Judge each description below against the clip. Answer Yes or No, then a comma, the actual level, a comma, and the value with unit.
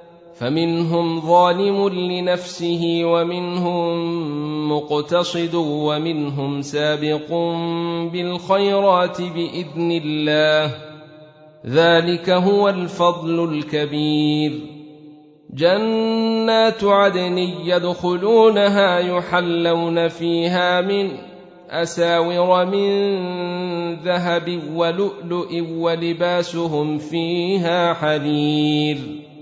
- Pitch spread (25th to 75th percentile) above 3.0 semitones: No, narrow, 2.6 semitones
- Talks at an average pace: No, slow, 55 wpm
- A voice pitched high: No, medium, 170 Hz